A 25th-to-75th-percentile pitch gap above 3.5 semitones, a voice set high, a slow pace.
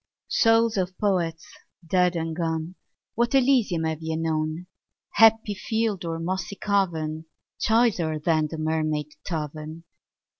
No: average, 4.2 semitones; medium, 165 Hz; slow, 120 wpm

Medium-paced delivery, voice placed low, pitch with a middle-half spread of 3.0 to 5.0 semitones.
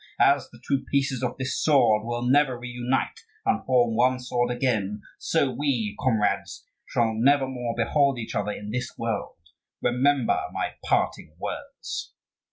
No: average, 145 wpm; low, 125 Hz; narrow, 2.6 semitones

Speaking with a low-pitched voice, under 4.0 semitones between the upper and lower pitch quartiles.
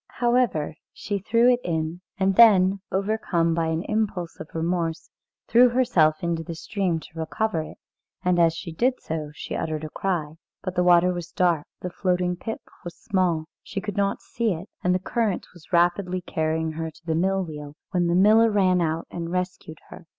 No: medium, 180 Hz; average, 3.4 semitones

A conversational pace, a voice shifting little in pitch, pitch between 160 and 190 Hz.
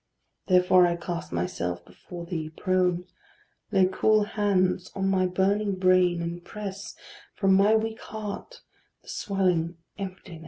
No: slow, 130 wpm; narrow, 2.3 semitones; medium, 185 Hz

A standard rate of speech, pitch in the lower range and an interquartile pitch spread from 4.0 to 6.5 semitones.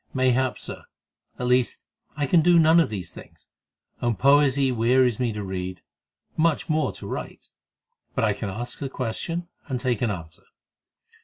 Yes: average, 165 wpm; low, 125 Hz; average, 4.4 semitones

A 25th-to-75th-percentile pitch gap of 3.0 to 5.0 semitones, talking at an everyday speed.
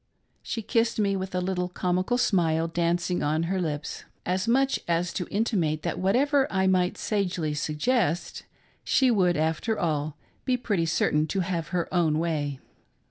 Yes: average, 3.7 semitones; average, 160 wpm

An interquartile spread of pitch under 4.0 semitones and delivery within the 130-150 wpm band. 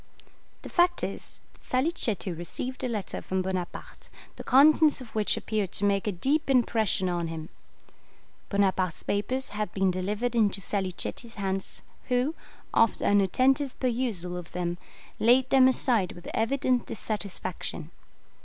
No: average, 5.3 semitones; average, 140 wpm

